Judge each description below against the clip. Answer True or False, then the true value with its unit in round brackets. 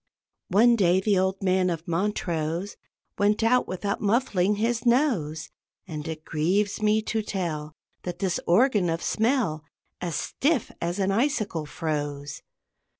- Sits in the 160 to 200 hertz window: True (190 Hz)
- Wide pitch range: False (4.6 semitones)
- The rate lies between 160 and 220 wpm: False (140 wpm)